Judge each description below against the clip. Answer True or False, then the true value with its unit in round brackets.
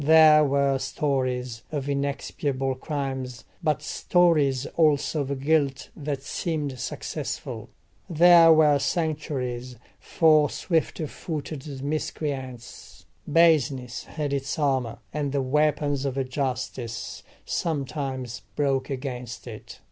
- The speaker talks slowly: True (100 wpm)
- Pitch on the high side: False (140 Hz)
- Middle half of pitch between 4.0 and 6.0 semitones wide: False (2.6 semitones)